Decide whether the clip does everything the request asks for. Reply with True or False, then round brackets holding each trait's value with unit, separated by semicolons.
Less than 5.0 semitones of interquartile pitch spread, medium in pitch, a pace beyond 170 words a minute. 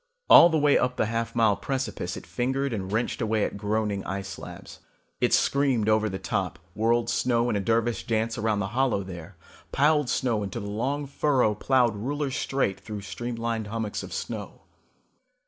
False (3.6 semitones; 115 Hz; 180 wpm)